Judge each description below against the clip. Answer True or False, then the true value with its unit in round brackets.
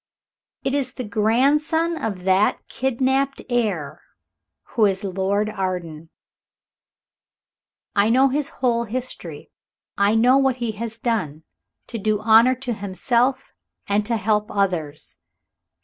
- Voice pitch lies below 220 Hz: False (225 Hz)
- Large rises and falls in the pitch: False (4.3 semitones)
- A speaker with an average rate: False (120 wpm)